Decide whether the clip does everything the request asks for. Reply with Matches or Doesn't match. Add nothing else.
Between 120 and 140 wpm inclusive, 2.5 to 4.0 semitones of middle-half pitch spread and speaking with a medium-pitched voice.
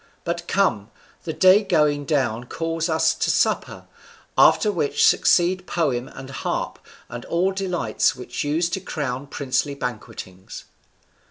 Doesn't match